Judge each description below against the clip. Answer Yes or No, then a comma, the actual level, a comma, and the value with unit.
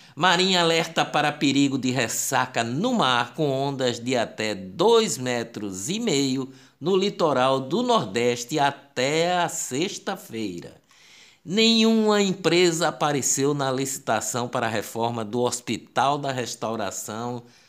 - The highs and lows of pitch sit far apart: Yes, wide, 5.9 semitones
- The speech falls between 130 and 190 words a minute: No, slow, 120 wpm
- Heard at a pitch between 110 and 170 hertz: Yes, medium, 140 Hz